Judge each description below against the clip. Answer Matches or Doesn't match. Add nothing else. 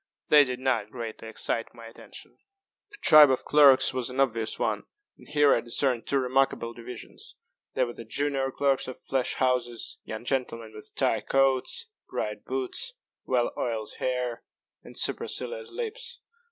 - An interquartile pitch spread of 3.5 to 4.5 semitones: Doesn't match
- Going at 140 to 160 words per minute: Matches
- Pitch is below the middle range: Matches